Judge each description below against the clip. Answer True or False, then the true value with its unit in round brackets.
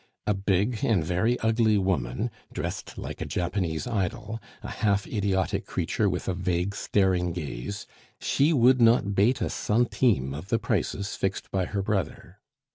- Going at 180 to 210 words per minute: False (155 wpm)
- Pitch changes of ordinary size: True (3.8 semitones)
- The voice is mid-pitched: False (100 Hz)